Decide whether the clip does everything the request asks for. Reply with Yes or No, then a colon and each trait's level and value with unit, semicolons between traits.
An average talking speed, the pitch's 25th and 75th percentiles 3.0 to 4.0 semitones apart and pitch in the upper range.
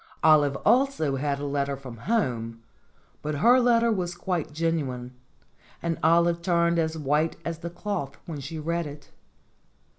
No: average, 150 wpm; average, 3.4 semitones; medium, 160 Hz